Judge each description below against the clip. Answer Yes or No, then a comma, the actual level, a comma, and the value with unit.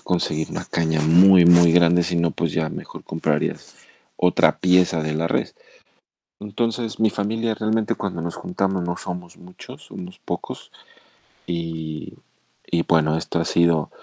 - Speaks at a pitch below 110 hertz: Yes, very low, 85 Hz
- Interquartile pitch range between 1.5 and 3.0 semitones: Yes, narrow, 2.5 semitones